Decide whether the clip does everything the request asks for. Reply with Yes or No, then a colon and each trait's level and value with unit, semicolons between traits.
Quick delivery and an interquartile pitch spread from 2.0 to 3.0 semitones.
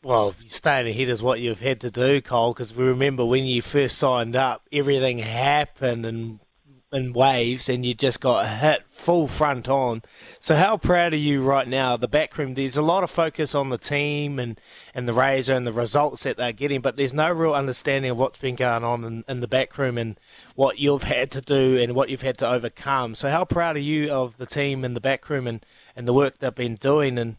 Yes: fast, 230 wpm; narrow, 2.5 semitones